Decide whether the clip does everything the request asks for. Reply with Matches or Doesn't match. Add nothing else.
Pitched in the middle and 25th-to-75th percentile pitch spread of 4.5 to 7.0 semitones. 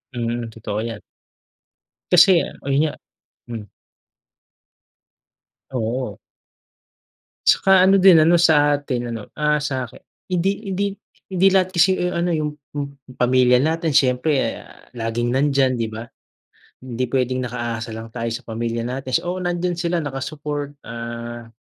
Doesn't match